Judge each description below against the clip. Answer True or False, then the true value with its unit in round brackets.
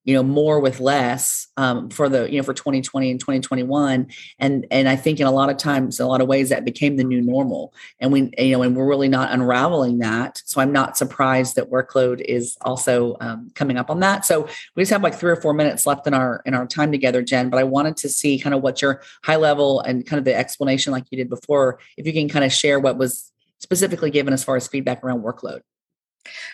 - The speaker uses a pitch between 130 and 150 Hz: True (135 Hz)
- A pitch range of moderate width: False (2.0 semitones)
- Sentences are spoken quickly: True (245 wpm)